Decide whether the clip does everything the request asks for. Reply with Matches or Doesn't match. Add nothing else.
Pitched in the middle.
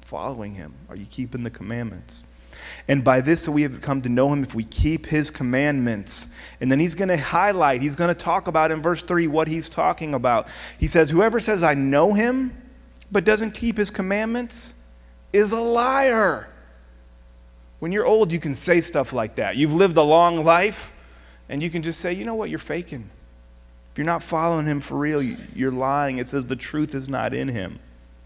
Matches